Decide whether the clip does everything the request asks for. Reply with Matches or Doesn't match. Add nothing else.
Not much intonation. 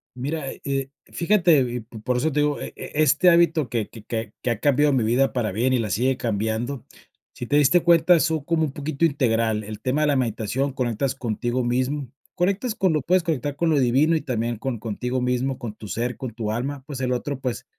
Doesn't match